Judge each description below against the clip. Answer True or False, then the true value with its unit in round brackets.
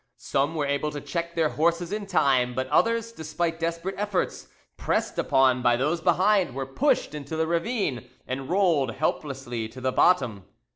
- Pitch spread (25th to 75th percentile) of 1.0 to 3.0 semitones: False (4.8 semitones)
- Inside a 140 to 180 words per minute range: True (165 wpm)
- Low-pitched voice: False (160 Hz)